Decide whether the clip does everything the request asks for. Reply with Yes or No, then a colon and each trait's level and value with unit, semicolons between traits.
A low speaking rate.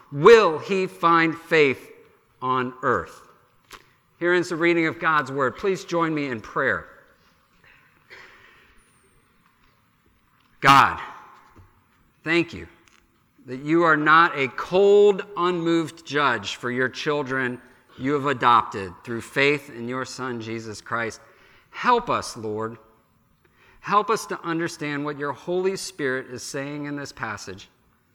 Yes: slow, 125 wpm